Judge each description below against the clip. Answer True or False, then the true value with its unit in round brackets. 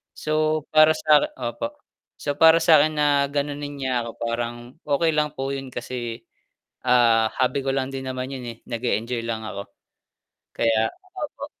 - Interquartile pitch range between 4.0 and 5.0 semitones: True (4.3 semitones)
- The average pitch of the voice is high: False (135 Hz)